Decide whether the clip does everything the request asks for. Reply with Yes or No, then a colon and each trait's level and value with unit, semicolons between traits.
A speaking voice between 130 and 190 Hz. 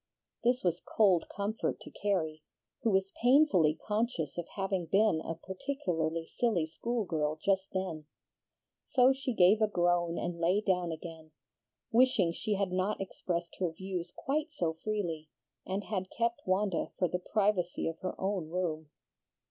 Yes: medium, 185 Hz